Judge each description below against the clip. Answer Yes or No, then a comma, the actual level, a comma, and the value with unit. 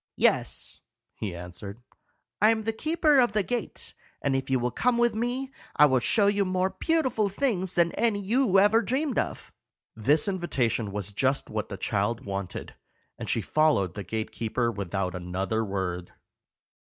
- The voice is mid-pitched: Yes, medium, 150 Hz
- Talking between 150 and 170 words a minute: Yes, average, 165 wpm